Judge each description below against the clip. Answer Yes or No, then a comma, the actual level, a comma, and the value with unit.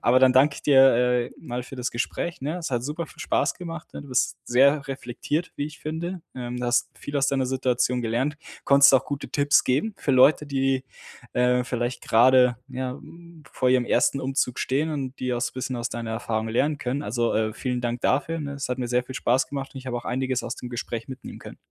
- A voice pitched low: Yes, low, 130 Hz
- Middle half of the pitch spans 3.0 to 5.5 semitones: No, narrow, 2.6 semitones